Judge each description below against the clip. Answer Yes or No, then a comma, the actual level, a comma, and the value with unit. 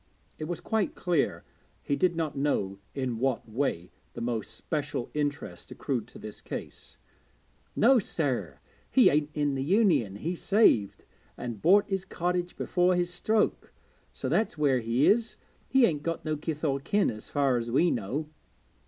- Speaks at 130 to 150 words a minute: No, average, 165 wpm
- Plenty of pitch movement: Yes, wide, 6.1 semitones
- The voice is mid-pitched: Yes, medium, 150 Hz